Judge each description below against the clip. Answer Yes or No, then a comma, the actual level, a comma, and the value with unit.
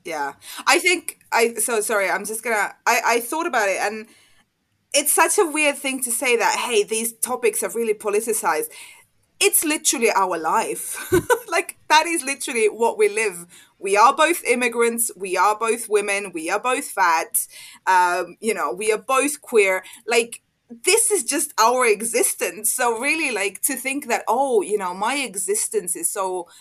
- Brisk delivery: No, average, 175 wpm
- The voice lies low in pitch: No, very high, 270 Hz